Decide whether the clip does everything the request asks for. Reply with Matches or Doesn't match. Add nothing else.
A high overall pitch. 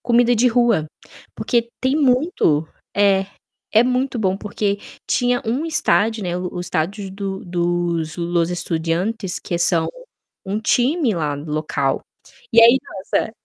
Matches